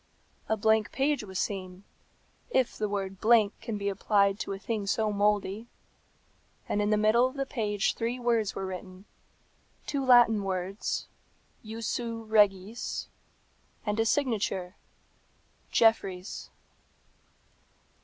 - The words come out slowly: Yes, slow, 125 wpm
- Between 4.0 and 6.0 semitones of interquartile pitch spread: No, average, 2.7 semitones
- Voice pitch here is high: Yes, high, 210 Hz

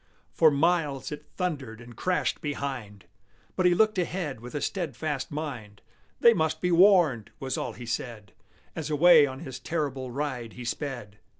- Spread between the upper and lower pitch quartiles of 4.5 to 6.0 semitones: Yes, average, 5.3 semitones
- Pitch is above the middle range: No, medium, 145 Hz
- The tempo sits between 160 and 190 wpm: Yes, average, 165 wpm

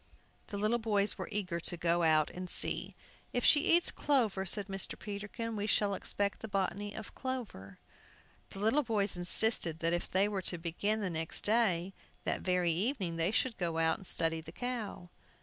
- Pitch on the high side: Yes, high, 200 Hz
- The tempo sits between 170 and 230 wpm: Yes, average, 185 wpm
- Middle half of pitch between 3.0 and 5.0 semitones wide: Yes, average, 4.1 semitones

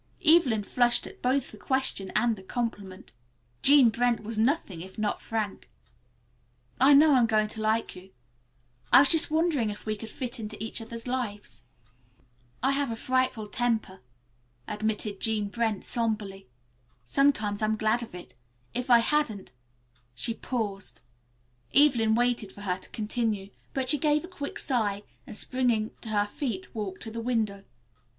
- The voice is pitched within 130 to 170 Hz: No, high, 225 Hz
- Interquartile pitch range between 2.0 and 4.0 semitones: Yes, average, 3.3 semitones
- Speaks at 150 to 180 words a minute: Yes, average, 160 wpm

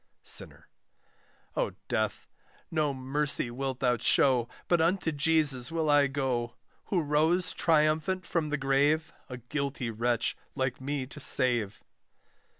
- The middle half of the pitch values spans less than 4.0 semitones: Yes, average, 3.6 semitones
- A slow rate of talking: Yes, slow, 130 wpm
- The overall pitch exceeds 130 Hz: Yes, medium, 140 Hz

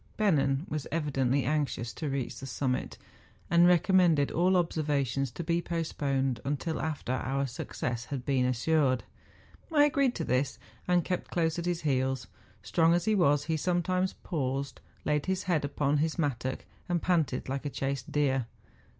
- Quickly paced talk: No, average, 165 wpm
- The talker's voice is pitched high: No, medium, 145 Hz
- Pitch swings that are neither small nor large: Yes, average, 4.2 semitones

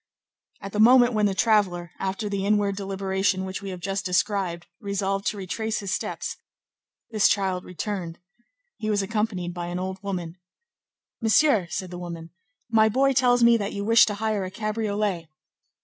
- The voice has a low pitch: No, high, 200 Hz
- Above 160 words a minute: Yes, average, 170 wpm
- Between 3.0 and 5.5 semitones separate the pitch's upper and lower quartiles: No, narrow, 2.5 semitones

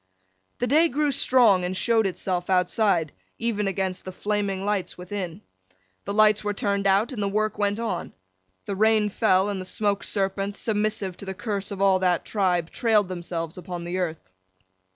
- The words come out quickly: No, average, 175 wpm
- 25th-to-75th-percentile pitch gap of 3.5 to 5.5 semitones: No, narrow, 2.5 semitones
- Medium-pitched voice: No, high, 200 Hz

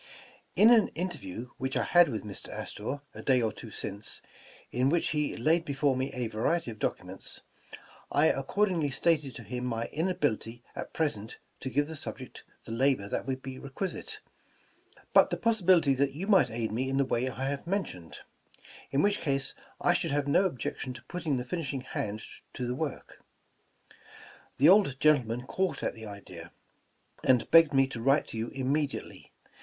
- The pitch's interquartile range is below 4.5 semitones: No, average, 4.8 semitones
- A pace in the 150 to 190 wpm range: Yes, average, 180 wpm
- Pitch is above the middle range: No, low, 135 Hz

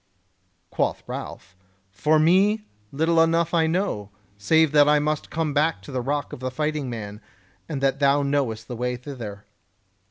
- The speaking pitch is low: No, medium, 145 Hz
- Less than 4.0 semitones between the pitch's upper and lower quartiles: No, average, 4.3 semitones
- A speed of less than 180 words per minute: Yes, average, 160 wpm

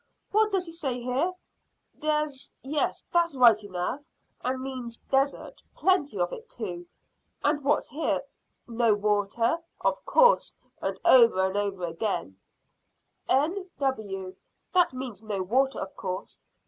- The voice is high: Yes, very high, 255 Hz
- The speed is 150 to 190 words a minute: No, slow, 135 wpm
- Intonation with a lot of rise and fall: Yes, wide, 6.6 semitones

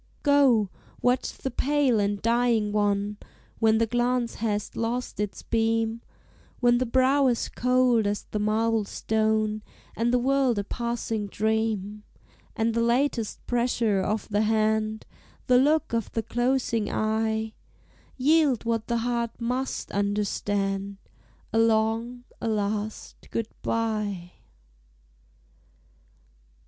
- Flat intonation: Yes, narrow, 2.3 semitones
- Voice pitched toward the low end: No, high, 225 Hz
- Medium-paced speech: No, slow, 120 wpm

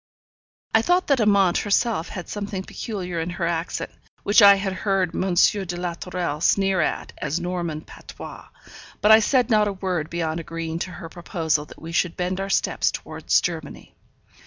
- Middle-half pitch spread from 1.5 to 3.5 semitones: Yes, average, 3.1 semitones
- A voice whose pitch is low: No, medium, 180 Hz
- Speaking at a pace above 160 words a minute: Yes, average, 180 wpm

